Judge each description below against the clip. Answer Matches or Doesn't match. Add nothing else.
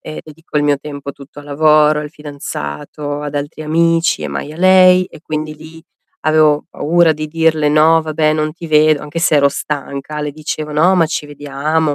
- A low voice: Doesn't match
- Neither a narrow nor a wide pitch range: Doesn't match